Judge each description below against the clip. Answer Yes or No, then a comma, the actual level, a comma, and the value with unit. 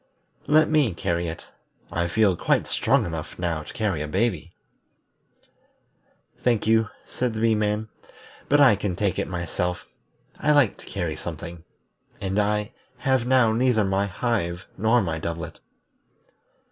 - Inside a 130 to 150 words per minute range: Yes, average, 145 wpm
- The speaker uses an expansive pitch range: No, average, 5.0 semitones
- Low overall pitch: Yes, low, 100 Hz